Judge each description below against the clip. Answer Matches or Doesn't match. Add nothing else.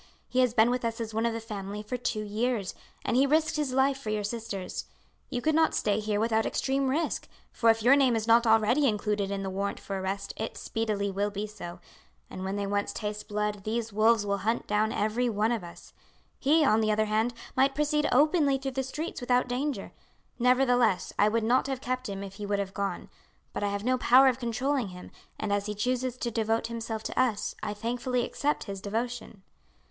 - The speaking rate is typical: Doesn't match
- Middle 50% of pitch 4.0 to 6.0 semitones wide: Doesn't match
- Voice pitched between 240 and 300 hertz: Doesn't match